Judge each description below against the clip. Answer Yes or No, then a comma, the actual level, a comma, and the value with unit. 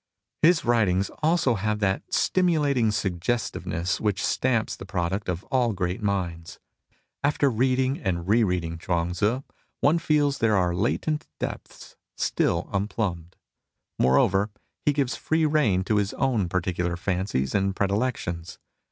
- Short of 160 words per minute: Yes, slow, 135 wpm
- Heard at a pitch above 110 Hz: No, low, 100 Hz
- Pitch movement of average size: No, wide, 6.1 semitones